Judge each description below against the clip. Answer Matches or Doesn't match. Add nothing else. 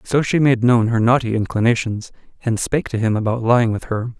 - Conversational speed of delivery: Doesn't match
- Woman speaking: Doesn't match